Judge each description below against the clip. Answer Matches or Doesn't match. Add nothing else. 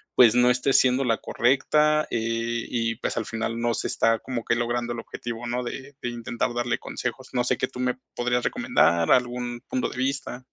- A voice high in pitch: Doesn't match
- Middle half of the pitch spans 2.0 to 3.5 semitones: Doesn't match